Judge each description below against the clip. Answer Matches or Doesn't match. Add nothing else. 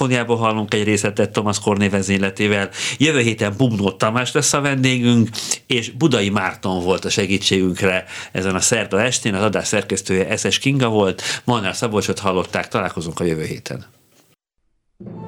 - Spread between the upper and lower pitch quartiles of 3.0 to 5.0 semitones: Matches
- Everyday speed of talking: Matches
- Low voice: Matches